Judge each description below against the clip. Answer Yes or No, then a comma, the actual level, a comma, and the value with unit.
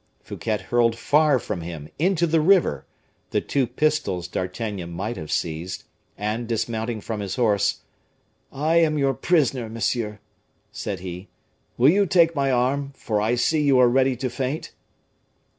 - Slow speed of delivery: No, average, 155 wpm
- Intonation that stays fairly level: No, wide, 5.5 semitones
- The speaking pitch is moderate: No, low, 120 Hz